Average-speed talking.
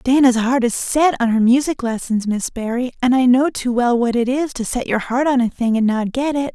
No: fast, 265 wpm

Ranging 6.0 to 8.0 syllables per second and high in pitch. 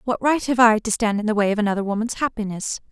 Yes: 6.6 syllables/s; high, 220 Hz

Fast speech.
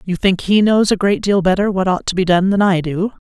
Yes: fast, 295 wpm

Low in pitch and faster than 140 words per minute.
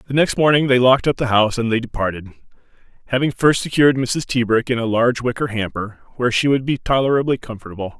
Yes: low, 120 Hz; fast, 205 wpm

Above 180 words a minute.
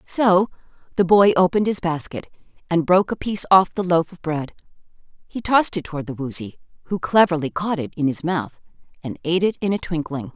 Yes: average, 195 wpm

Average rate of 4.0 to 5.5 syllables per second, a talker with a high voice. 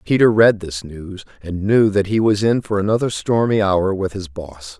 No: 4.7 syllables/s; low, 100 Hz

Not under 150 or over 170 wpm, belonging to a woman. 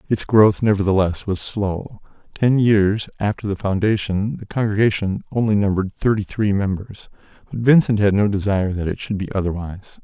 No: average, 160 wpm; male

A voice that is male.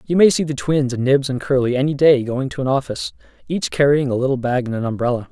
Yes: male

